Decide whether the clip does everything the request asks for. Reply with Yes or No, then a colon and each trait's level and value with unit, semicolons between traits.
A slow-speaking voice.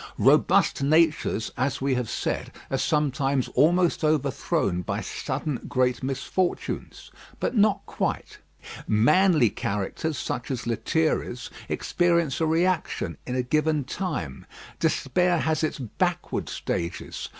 Yes: slow, 115 wpm